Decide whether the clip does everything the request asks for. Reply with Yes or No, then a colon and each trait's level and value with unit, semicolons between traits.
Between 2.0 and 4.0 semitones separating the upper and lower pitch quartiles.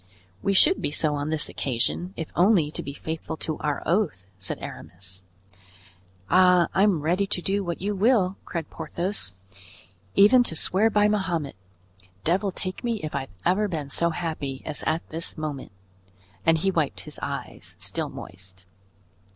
No: average, 4.6 semitones